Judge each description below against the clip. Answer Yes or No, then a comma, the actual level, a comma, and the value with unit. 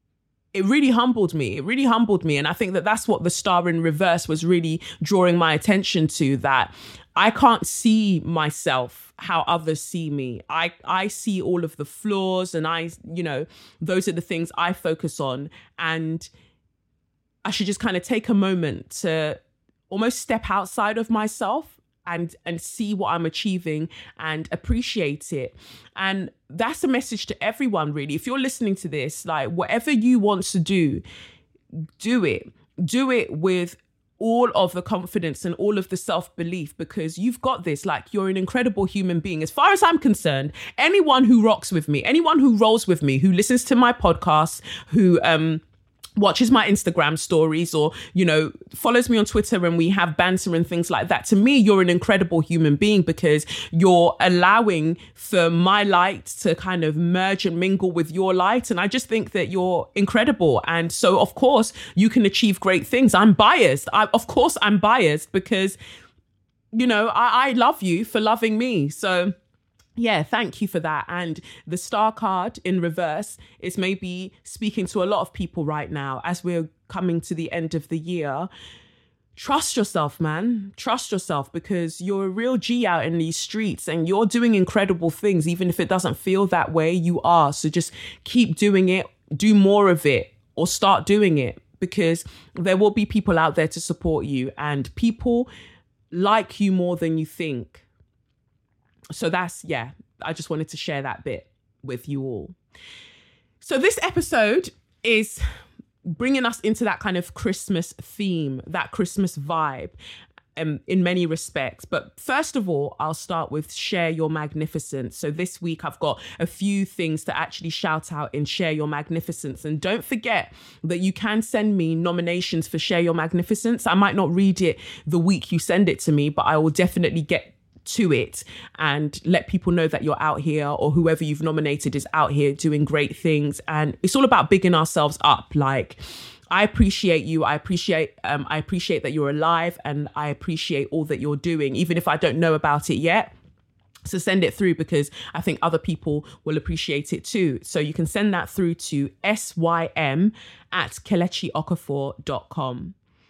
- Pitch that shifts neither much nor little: Yes, average, 4.5 semitones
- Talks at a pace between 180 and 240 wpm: Yes, average, 185 wpm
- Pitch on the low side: No, medium, 175 Hz